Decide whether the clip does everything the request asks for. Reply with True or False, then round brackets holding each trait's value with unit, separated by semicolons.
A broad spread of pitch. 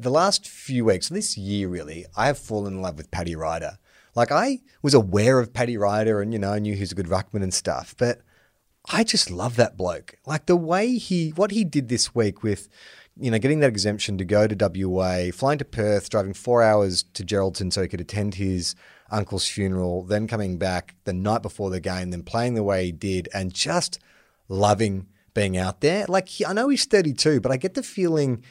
True (5.8 semitones)